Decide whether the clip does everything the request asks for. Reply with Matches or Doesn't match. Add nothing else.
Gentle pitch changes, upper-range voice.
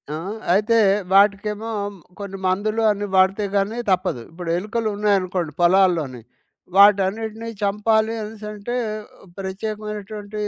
Matches